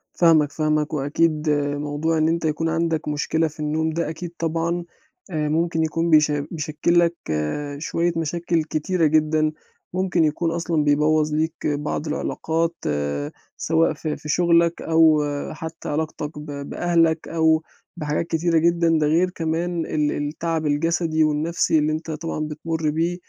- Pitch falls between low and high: Yes, medium, 160 Hz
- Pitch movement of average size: No, narrow, 1.6 semitones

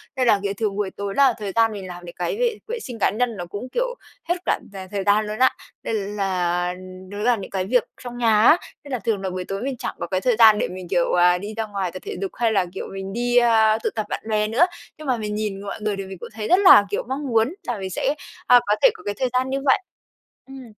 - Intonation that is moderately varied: Yes, average, 4.0 semitones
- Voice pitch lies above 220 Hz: No, high, 215 Hz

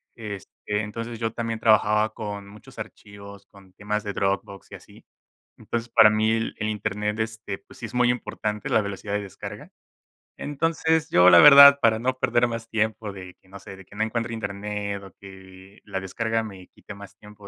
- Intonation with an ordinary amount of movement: No, narrow, 2.3 semitones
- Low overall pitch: Yes, low, 105 Hz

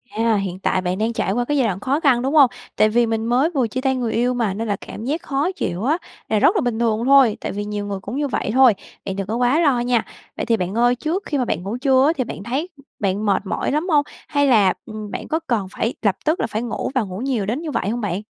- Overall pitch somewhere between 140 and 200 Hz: No, high, 235 Hz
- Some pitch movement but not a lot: Yes, average, 4.6 semitones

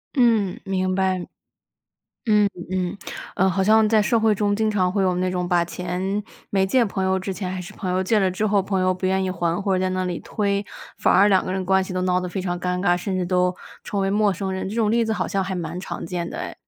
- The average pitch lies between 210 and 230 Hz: No, high, 190 Hz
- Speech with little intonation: Yes, narrow, 1.9 semitones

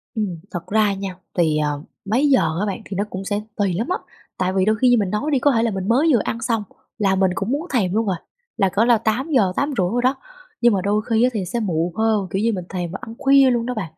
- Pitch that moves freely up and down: No, average, 4.1 semitones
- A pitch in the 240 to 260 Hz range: No, high, 210 Hz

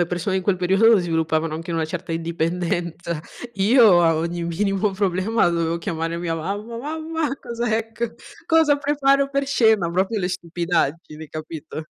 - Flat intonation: No, average, 5.2 semitones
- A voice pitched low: No, medium, 180 Hz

